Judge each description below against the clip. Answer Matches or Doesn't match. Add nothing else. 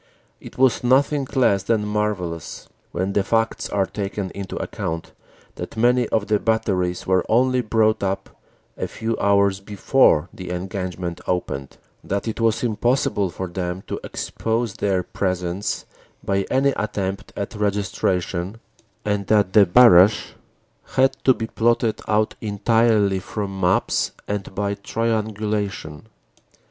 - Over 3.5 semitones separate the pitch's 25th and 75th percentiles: Doesn't match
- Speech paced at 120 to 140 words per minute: Matches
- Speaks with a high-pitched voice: Doesn't match